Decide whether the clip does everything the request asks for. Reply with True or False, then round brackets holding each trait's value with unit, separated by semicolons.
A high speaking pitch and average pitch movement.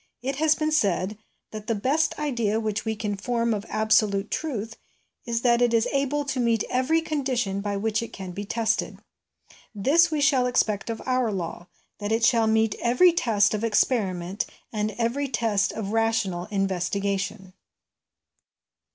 True (225 Hz; 3.7 semitones)